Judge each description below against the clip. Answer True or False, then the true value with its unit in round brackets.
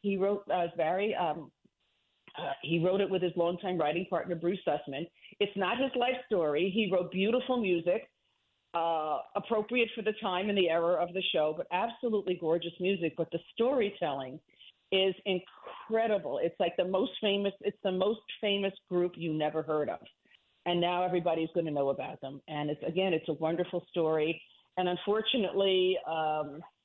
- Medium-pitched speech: True (180 Hz)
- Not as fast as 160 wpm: False (175 wpm)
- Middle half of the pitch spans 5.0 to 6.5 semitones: False (3.3 semitones)